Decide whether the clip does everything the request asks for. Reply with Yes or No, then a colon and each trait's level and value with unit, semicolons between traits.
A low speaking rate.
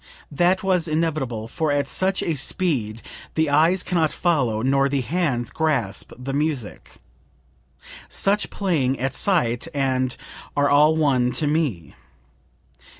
Yes: slow, 125 wpm